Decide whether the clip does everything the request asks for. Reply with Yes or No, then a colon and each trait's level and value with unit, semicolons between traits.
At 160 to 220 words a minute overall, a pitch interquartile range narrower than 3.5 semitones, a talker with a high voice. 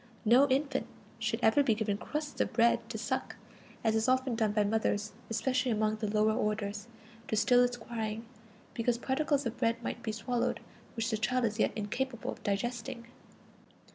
Yes: average, 175 wpm; average, 2.7 semitones; high, 230 Hz